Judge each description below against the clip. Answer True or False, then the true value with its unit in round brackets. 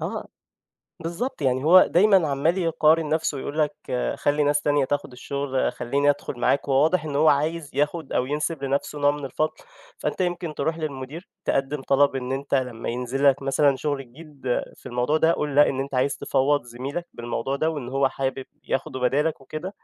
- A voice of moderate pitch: True (145 Hz)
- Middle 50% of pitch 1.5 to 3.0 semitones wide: True (2.6 semitones)